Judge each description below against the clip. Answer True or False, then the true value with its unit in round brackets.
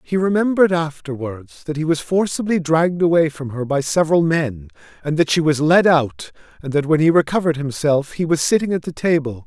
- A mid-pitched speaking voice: True (155 Hz)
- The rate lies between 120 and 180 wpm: False (205 wpm)